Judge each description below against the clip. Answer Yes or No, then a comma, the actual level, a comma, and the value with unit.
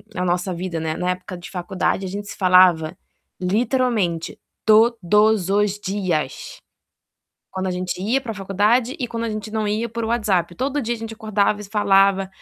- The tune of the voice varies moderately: Yes, average, 3.4 semitones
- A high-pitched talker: Yes, high, 200 Hz